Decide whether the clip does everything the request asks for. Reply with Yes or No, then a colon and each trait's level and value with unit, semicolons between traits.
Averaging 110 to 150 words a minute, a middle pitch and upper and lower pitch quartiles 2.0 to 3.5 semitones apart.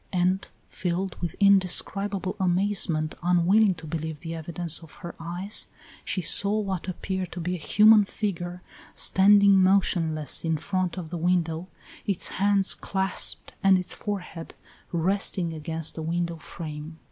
Yes: average, 140 wpm; medium, 180 Hz; average, 2.8 semitones